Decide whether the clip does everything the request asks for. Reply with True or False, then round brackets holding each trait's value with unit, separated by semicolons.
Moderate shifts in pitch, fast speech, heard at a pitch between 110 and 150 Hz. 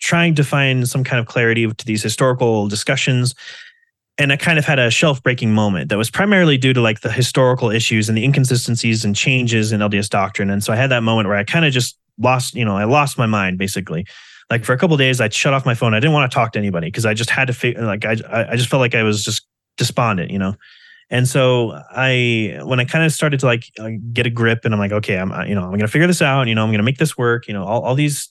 True (3.5 semitones; 280 wpm; 120 Hz)